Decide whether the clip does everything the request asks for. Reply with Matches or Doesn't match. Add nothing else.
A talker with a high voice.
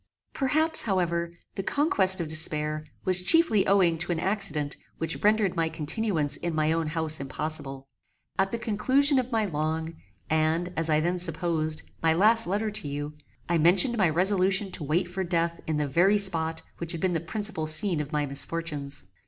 Doesn't match